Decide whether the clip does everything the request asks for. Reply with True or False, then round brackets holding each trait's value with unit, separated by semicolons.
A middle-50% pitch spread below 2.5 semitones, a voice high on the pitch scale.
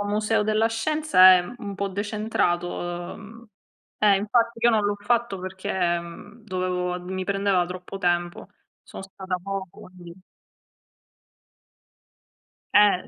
False (2.9 semitones; 195 Hz)